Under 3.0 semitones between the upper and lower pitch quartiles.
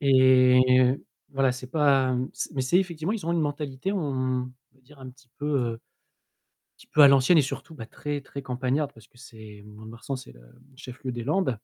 Yes: narrow, 2.5 semitones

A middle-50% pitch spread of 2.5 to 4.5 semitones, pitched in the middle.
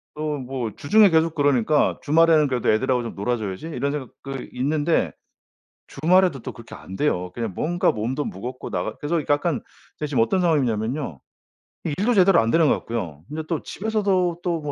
No: wide, 5.5 semitones; medium, 145 Hz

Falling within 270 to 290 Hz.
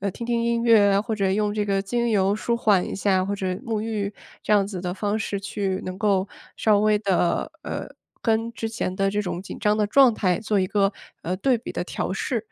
No: high, 205 Hz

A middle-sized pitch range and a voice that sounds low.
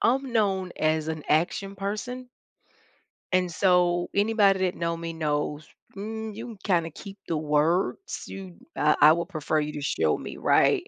No: average, 4.3 semitones; medium, 175 Hz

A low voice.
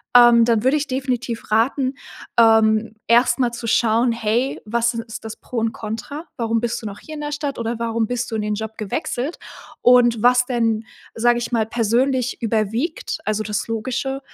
No: high, 235 Hz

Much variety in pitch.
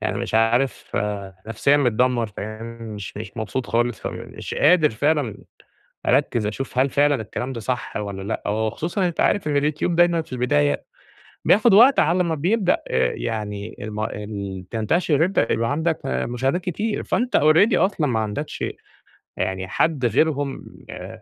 Yes: wide, 6.7 semitones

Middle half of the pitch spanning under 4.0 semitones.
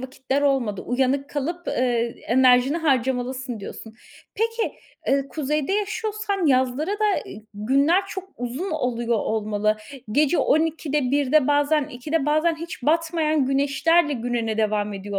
No: average, 4.6 semitones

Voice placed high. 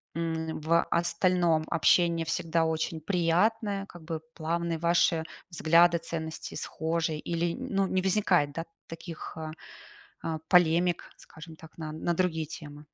No: medium, 165 Hz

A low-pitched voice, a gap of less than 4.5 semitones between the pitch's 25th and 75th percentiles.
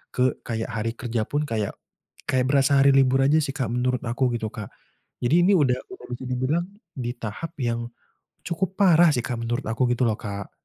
Yes: low, 125 Hz; average, 3.1 semitones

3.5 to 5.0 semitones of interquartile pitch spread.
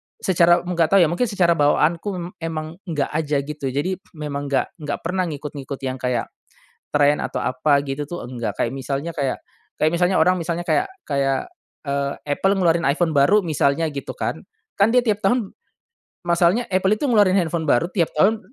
Yes: average, 4.1 semitones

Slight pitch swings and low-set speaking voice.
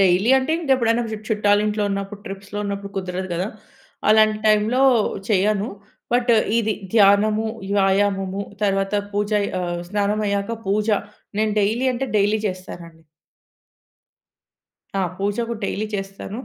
No: narrow, 1.7 semitones; high, 205 Hz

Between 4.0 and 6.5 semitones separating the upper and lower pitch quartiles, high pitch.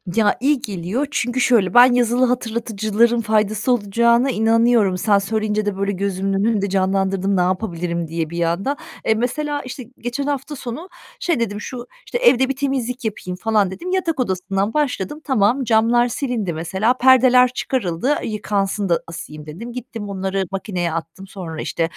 Yes: average, 4.5 semitones; high, 220 Hz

